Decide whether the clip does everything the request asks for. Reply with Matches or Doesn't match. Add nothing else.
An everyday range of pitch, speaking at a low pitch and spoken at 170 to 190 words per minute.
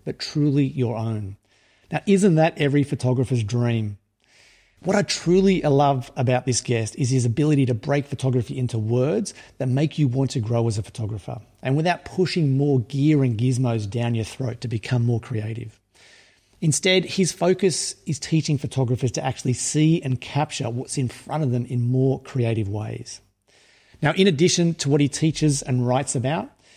Matches